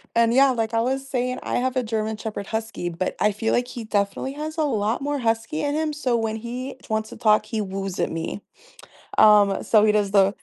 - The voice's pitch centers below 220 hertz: No, high, 225 Hz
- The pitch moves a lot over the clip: No, average, 3.4 semitones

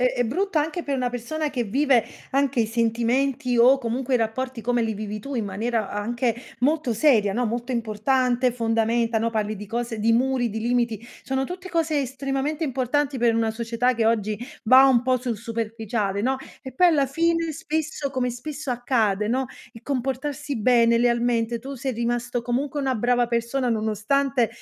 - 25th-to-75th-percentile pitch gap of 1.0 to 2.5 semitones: No, average, 2.9 semitones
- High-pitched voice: Yes, high, 245 Hz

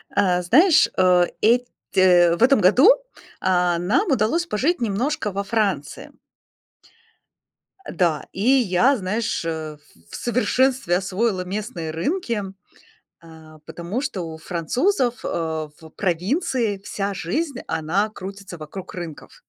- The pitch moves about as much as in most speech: No, wide, 5.9 semitones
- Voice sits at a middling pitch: No, high, 195 Hz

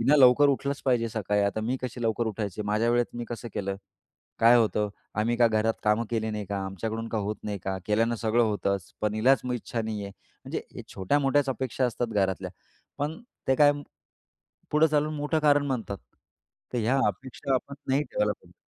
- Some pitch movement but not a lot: Yes, average, 3.9 semitones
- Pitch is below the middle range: Yes, low, 115 Hz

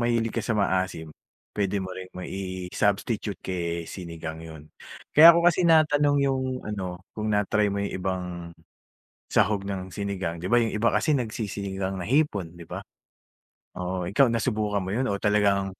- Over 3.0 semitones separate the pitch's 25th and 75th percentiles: Yes, average, 3.6 semitones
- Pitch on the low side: Yes, low, 100 Hz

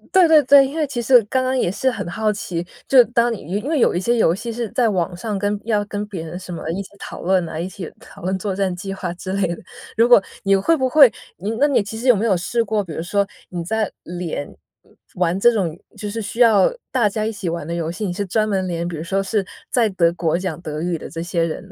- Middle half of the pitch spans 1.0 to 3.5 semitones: No, average, 4.4 semitones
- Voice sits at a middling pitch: No, high, 200 Hz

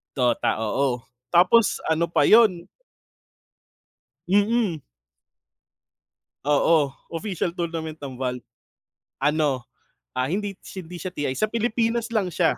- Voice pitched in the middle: Yes, medium, 170 Hz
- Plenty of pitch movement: Yes, wide, 6.4 semitones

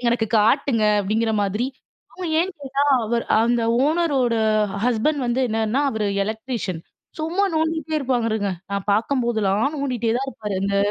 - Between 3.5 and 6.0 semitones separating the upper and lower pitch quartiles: Yes, average, 4.3 semitones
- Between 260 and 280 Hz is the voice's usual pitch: No, high, 235 Hz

